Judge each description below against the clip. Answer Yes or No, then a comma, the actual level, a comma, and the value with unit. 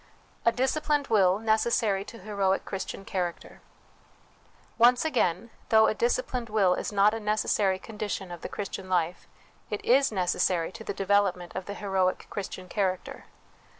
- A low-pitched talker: No, high, 200 Hz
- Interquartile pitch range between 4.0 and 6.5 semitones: No, average, 3.0 semitones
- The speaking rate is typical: Yes, average, 150 wpm